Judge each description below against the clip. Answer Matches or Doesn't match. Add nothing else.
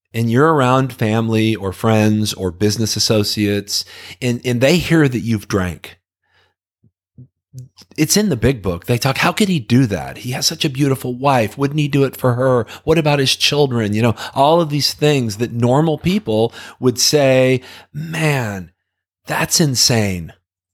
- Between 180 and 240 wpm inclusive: Doesn't match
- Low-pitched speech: Matches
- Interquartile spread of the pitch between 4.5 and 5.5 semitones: Matches